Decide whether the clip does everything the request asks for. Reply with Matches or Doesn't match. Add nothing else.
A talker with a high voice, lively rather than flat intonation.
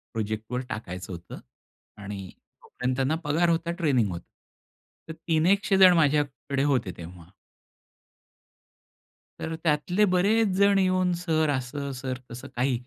Doesn't match